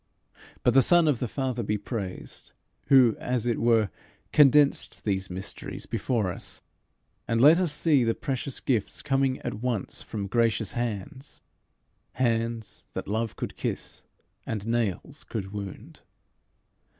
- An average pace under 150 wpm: Yes, average, 140 wpm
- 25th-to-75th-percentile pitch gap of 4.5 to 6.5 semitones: No, average, 3.9 semitones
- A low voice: Yes, low, 115 Hz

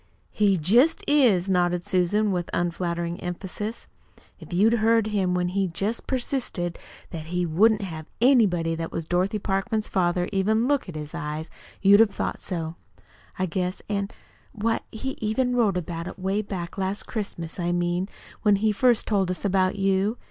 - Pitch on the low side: No, high, 190 Hz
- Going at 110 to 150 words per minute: No, average, 170 wpm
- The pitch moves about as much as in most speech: Yes, average, 3.5 semitones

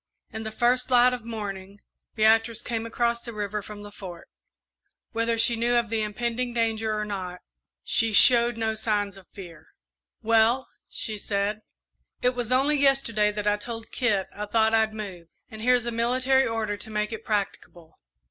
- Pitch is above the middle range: Yes, high, 220 Hz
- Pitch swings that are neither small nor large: No, narrow, 2.3 semitones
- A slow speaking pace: No, average, 175 wpm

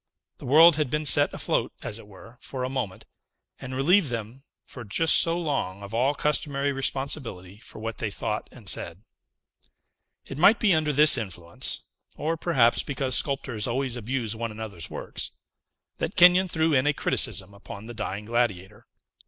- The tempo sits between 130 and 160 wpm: No, average, 170 wpm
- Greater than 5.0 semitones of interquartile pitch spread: Yes, wide, 5.5 semitones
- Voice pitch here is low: Yes, low, 125 Hz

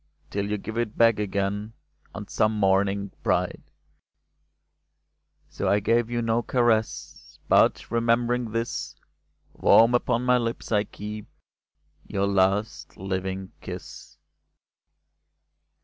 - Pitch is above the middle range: No, low, 110 Hz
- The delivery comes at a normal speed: No, slow, 110 wpm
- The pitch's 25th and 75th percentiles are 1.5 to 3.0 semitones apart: Yes, average, 2.7 semitones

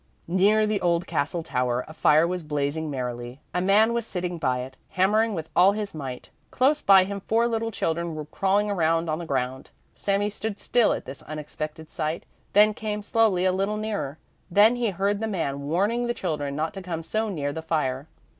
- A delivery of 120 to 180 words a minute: No, average, 200 wpm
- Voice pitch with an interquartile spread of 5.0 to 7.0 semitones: Yes, average, 5.3 semitones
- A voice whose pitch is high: No, medium, 180 Hz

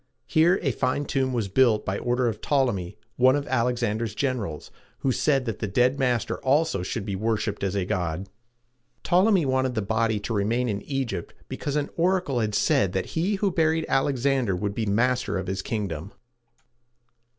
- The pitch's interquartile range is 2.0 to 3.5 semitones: No, average, 5.0 semitones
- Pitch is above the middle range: No, low, 120 Hz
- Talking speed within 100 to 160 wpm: No, average, 180 wpm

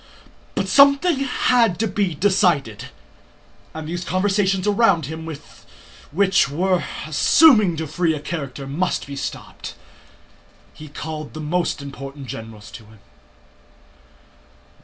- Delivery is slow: Yes, slow, 115 wpm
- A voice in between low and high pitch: Yes, medium, 165 Hz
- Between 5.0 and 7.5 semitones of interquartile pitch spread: Yes, wide, 5.5 semitones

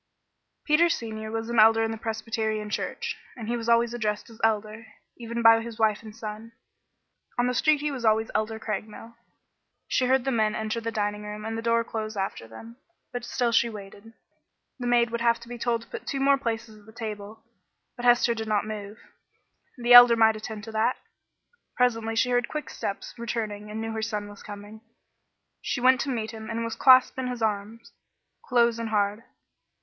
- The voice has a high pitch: Yes, high, 225 Hz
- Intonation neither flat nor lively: No, narrow, 1.7 semitones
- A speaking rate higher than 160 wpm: Yes, average, 200 wpm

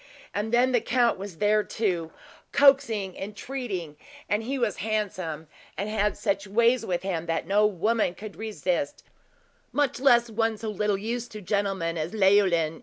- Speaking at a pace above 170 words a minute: No, average, 165 wpm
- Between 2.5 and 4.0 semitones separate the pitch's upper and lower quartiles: Yes, average, 3.4 semitones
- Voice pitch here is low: No, high, 210 Hz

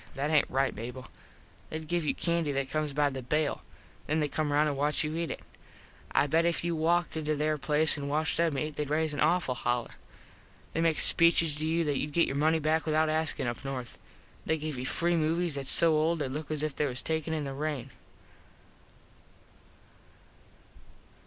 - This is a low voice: No, medium, 155 Hz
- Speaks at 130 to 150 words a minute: No, fast, 205 wpm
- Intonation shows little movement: Yes, narrow, 2.1 semitones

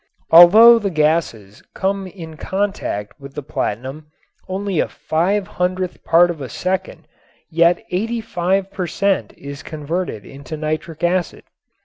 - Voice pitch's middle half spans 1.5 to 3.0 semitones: No, average, 3.8 semitones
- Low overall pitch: No, medium, 175 Hz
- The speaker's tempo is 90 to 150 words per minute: Yes, slow, 135 wpm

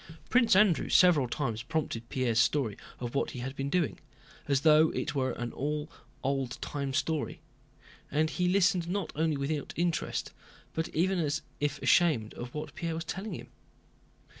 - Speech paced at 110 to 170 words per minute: Yes, average, 165 wpm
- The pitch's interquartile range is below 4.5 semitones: Yes, average, 4.0 semitones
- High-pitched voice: No, medium, 150 Hz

